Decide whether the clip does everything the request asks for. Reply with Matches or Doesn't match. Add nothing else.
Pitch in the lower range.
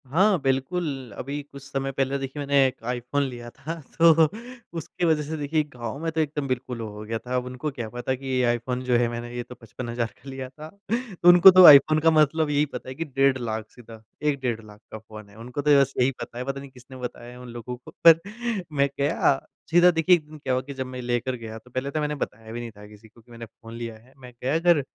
Matches